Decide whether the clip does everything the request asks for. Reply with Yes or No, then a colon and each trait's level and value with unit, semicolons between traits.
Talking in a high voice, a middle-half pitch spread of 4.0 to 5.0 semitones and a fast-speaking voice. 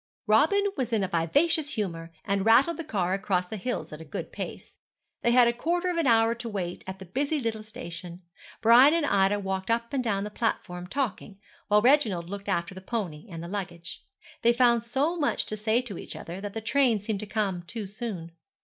Yes: high, 215 Hz; average, 4.5 semitones; fast, 215 wpm